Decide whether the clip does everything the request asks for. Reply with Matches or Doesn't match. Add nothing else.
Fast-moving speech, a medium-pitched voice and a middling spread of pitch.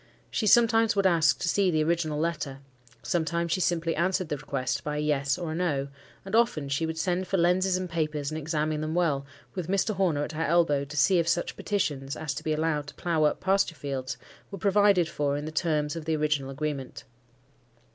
Matches